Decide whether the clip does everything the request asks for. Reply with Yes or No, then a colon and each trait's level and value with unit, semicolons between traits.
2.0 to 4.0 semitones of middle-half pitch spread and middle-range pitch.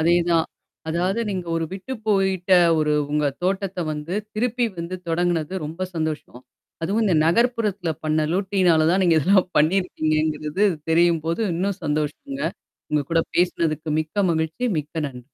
Yes: average, 3.4 semitones; medium, 170 Hz